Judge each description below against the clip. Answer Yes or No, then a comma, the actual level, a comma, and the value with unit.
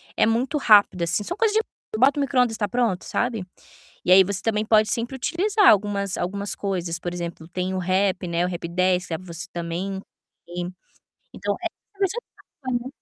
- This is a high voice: Yes, high, 195 Hz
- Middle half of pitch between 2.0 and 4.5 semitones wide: No, average, 5.2 semitones